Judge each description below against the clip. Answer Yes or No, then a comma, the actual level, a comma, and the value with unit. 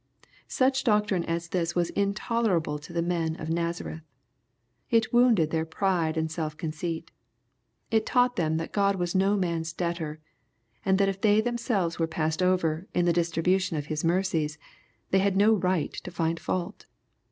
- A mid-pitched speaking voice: Yes, medium, 175 Hz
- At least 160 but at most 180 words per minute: Yes, average, 175 wpm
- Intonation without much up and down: No, average, 3.5 semitones